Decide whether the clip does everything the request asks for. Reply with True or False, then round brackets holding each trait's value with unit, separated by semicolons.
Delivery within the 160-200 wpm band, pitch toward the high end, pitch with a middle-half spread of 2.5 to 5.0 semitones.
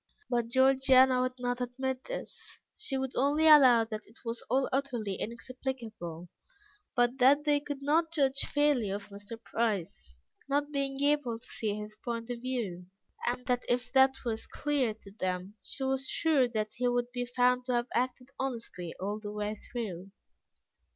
True (170 wpm; 245 Hz; 3.3 semitones)